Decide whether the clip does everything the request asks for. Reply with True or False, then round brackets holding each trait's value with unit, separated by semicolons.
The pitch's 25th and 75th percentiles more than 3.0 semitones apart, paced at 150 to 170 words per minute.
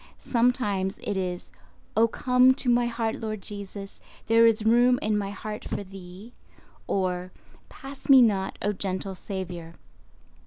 False (3.6 semitones; 140 wpm)